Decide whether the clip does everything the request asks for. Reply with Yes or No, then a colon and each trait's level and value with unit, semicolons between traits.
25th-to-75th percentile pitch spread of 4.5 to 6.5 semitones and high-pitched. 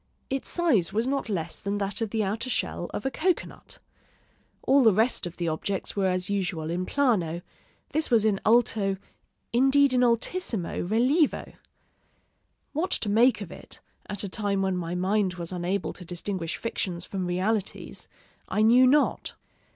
Yes: average, 5.0 semitones; high, 205 Hz